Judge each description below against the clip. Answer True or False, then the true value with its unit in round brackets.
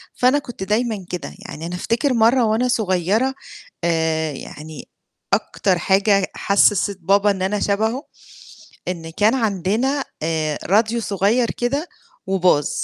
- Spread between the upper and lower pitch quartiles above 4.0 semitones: True (4.6 semitones)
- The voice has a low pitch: False (200 Hz)